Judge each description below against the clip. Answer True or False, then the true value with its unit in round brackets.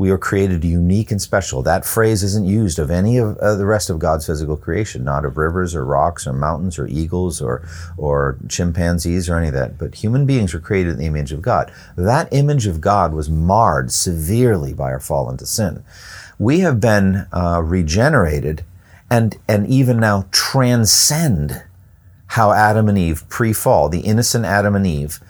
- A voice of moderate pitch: False (90 Hz)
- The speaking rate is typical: True (180 wpm)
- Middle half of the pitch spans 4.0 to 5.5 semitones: True (5.0 semitones)